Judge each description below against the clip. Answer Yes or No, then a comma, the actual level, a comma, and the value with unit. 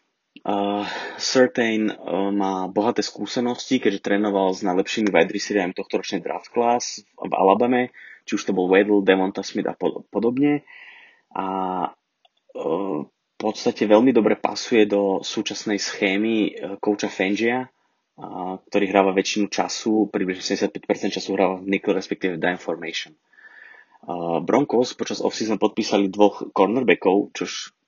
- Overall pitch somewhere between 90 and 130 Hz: Yes, low, 100 Hz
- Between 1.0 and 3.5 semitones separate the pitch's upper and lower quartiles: Yes, average, 2.7 semitones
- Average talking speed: Yes, average, 140 wpm